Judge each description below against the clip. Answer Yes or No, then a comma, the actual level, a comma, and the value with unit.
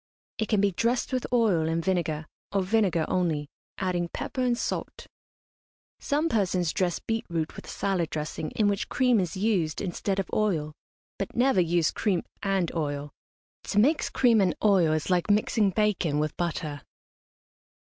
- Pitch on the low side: No, medium, 185 Hz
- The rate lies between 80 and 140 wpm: No, average, 165 wpm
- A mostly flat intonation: No, average, 4.5 semitones